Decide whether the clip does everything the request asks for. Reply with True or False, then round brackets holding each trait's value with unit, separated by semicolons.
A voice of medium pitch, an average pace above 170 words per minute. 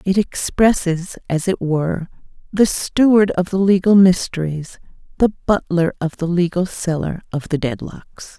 False (180 Hz; 145 wpm)